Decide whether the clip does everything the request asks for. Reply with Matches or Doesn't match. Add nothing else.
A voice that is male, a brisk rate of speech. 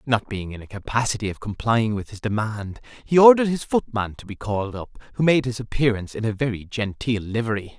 Matches